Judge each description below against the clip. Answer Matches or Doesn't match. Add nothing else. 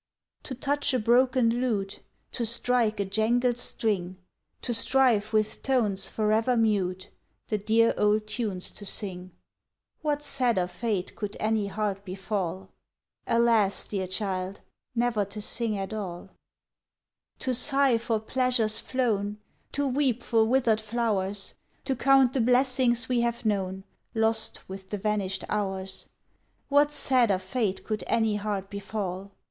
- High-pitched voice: Matches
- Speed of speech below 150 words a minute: Matches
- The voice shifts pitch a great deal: Doesn't match